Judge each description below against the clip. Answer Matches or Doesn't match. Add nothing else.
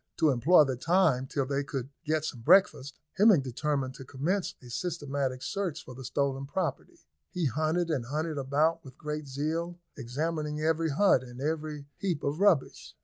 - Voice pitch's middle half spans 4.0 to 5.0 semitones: Doesn't match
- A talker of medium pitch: Matches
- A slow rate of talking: Doesn't match